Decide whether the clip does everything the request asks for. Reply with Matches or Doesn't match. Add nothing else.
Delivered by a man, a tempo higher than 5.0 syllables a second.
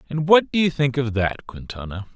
Matches